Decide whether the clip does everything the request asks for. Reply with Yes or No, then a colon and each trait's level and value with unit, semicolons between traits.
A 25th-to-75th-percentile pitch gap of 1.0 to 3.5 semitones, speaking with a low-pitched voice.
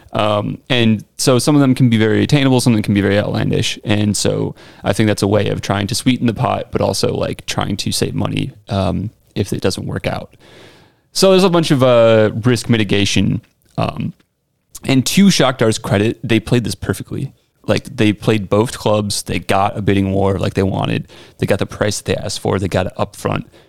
No: average, 4.0 semitones; low, 110 Hz